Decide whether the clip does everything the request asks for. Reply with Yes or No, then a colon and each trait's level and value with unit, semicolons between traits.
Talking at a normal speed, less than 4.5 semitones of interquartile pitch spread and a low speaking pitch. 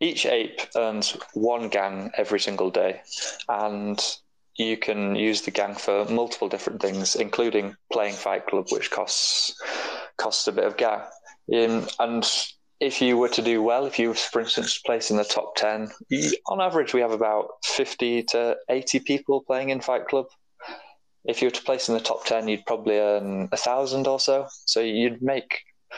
Yes: average, 180 wpm; average, 3.9 semitones; low, 115 Hz